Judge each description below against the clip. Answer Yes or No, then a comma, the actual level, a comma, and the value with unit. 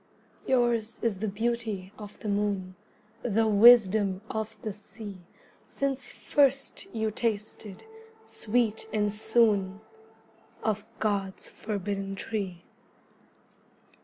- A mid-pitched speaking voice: No, high, 215 Hz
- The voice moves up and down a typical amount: No, narrow, 2.2 semitones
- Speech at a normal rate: No, slow, 100 wpm